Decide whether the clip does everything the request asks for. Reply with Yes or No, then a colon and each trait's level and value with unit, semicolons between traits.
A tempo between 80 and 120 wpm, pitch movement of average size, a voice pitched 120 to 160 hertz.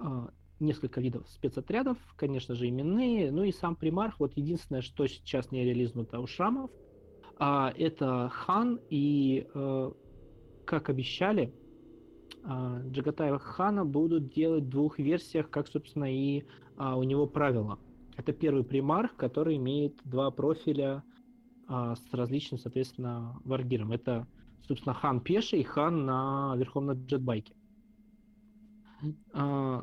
Yes: average, 115 wpm; average, 4.1 semitones; medium, 140 Hz